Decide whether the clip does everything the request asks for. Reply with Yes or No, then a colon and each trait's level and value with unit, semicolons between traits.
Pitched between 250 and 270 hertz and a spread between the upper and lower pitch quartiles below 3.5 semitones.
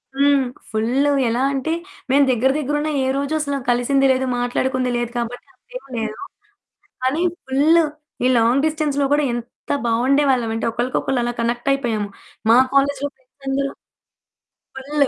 Yes: very high, 265 Hz; average, 2.8 semitones